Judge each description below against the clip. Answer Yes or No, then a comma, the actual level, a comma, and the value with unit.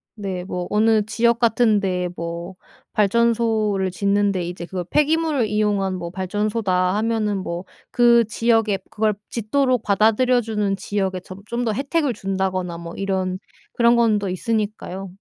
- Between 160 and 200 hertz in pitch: No, high, 210 Hz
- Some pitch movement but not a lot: Yes, average, 3.4 semitones